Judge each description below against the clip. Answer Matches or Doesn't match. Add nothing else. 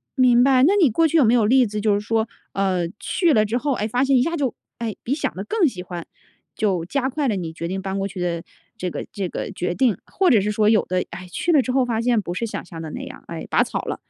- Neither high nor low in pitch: Doesn't match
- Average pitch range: Doesn't match